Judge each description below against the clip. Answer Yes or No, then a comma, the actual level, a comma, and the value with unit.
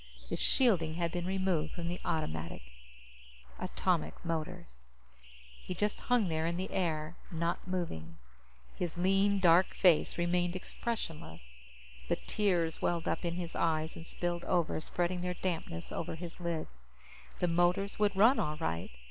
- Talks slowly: No, average, 145 wpm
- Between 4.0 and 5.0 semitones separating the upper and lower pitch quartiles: No, average, 2.8 semitones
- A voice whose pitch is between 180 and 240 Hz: No, medium, 170 Hz